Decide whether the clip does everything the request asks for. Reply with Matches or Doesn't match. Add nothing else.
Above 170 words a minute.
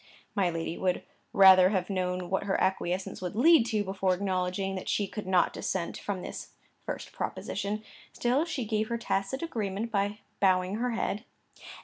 Doesn't match